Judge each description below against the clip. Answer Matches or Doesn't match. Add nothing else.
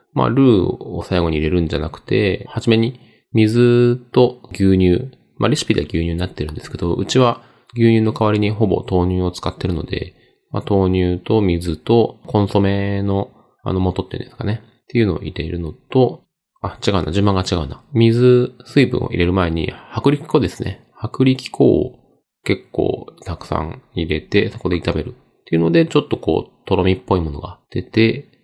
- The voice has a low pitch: Matches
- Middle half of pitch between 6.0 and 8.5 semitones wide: Doesn't match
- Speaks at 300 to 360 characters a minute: Matches